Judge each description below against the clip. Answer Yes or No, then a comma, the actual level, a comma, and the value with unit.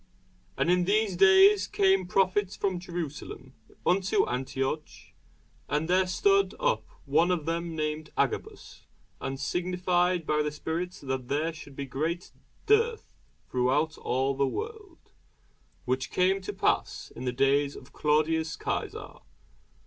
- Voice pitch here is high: No, medium, 165 Hz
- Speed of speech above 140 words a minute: No, slow, 135 wpm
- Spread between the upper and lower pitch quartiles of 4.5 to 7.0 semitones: Yes, average, 4.8 semitones